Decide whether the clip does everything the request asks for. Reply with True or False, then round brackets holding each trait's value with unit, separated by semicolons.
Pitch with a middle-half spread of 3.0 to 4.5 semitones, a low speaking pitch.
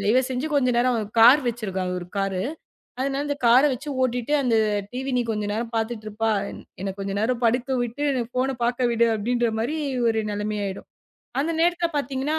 False (3.5 semitones; 240 Hz)